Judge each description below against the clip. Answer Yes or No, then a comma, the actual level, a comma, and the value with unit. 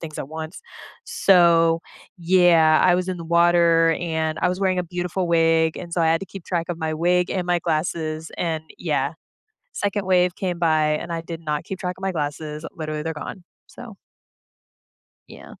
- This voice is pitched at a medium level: Yes, medium, 170 Hz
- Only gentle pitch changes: Yes, narrow, 2.0 semitones